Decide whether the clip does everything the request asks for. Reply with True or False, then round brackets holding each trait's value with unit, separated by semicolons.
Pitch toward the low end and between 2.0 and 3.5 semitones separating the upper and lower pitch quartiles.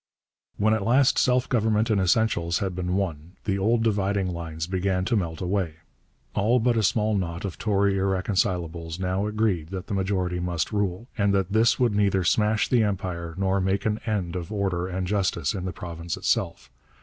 True (95 Hz; 3.0 semitones)